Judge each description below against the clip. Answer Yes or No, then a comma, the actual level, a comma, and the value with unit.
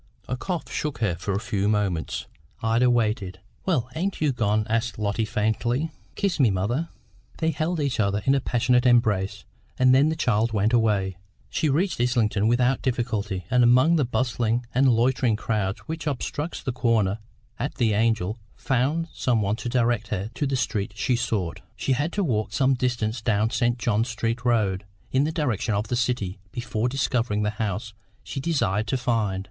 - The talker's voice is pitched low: Yes, low, 120 Hz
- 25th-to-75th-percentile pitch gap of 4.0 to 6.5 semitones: No, average, 3.6 semitones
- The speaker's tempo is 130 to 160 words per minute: No, average, 180 wpm